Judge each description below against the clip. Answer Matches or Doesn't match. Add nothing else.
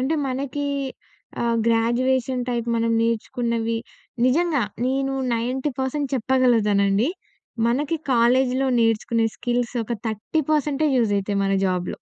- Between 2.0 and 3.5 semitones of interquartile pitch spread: Matches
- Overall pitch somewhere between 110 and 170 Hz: Doesn't match